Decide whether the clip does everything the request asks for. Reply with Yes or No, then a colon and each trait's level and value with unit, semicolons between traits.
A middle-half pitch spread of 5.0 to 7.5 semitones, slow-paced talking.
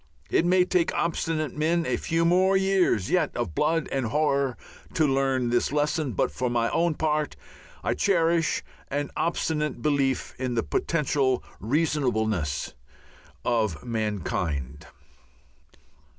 Yes: wide, 5.5 semitones; slow, 125 wpm